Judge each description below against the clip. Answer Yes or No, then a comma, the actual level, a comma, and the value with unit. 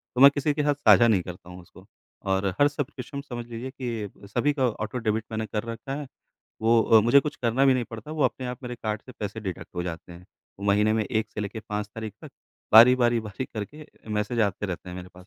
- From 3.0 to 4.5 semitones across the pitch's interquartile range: Yes, average, 3.7 semitones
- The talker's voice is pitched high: No, low, 110 Hz